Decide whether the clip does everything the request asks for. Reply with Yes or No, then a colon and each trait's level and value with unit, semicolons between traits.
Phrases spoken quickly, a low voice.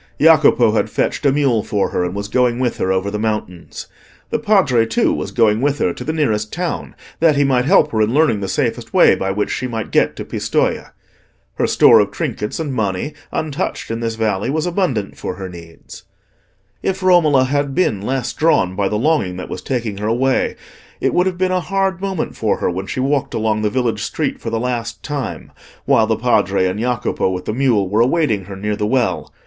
Yes: fast, 215 wpm; low, 120 Hz